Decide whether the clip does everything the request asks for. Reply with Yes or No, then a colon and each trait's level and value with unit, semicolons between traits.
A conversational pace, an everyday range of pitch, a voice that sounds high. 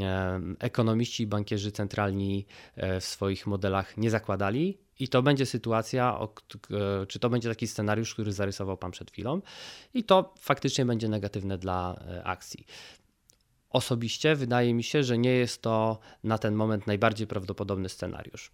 No: average, 140 wpm; average, 3.7 semitones; low, 110 Hz